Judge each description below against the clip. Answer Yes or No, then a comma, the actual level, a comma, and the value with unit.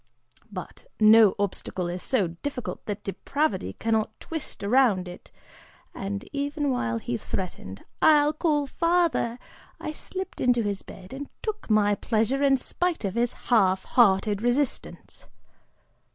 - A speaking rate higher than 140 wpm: No, slow, 135 wpm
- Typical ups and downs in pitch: No, wide, 6.5 semitones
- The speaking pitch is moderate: No, high, 225 Hz